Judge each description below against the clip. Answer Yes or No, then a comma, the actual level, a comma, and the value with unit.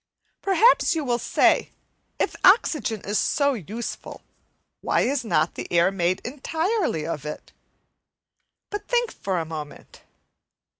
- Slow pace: Yes, slow, 130 wpm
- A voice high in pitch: Yes, high, 240 Hz